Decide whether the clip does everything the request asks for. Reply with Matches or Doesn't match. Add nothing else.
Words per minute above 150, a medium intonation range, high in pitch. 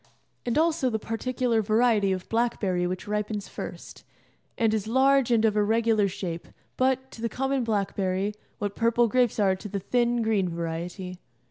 Matches